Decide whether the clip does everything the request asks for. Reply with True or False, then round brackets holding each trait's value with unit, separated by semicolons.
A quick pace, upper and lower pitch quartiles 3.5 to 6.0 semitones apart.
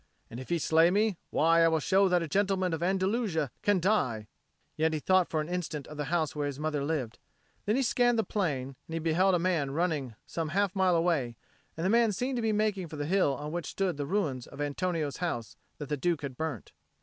True (235 wpm; 4.4 semitones)